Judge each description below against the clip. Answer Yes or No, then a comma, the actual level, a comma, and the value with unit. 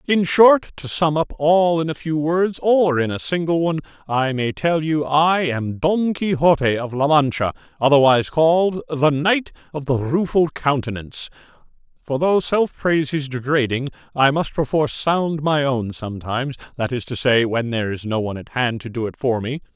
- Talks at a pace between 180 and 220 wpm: Yes, average, 190 wpm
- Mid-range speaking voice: Yes, medium, 145 Hz